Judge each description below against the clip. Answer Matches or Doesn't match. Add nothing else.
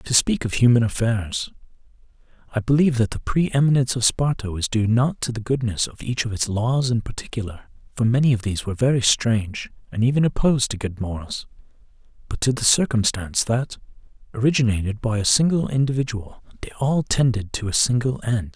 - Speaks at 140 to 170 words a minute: Doesn't match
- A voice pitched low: Matches